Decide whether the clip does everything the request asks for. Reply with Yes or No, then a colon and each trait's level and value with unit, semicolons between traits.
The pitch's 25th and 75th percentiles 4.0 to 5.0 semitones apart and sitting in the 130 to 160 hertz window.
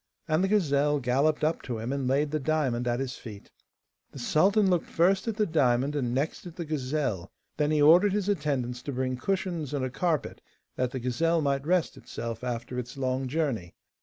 Yes: average, 4.4 semitones; medium, 140 Hz